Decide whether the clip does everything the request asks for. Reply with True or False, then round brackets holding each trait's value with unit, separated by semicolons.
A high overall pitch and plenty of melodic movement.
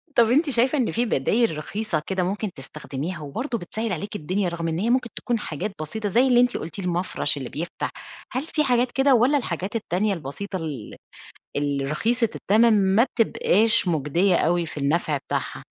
True (195 Hz; 6.4 semitones)